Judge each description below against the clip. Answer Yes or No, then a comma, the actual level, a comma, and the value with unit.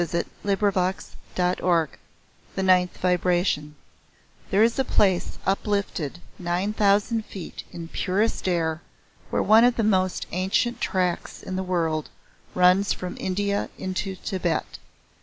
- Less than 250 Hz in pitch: Yes, medium, 185 Hz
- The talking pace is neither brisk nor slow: No, slow, 130 wpm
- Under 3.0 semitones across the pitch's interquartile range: Yes, narrow, 2.4 semitones